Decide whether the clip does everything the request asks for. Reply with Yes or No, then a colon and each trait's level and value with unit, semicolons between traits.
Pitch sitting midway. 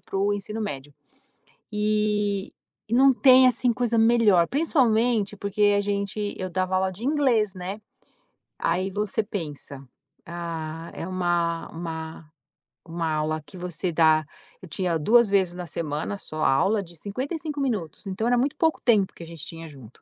No: high, 195 Hz